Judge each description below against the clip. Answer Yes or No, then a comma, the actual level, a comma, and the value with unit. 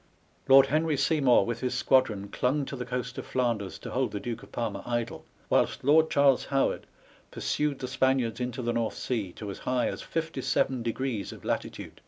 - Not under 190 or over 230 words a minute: Yes, average, 195 wpm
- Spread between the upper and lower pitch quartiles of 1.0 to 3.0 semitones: Yes, narrow, 2.6 semitones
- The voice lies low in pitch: Yes, low, 125 Hz